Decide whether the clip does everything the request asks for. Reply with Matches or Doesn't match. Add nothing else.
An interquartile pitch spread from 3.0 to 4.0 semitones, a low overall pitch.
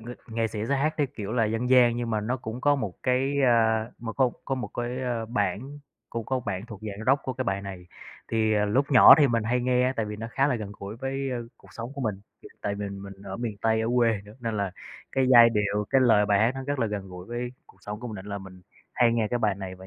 Matches